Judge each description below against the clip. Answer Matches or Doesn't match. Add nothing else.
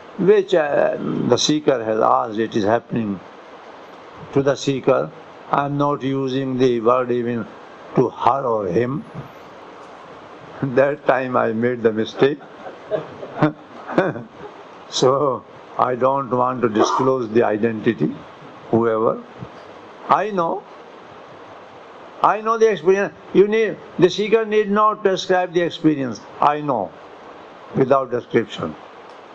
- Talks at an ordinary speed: Doesn't match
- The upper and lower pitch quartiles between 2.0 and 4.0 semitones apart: Doesn't match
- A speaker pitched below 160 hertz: Matches